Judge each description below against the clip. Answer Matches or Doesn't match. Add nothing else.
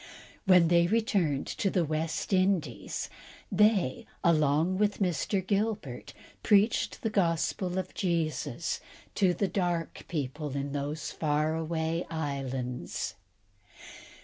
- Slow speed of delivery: Matches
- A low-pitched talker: Doesn't match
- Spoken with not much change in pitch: Doesn't match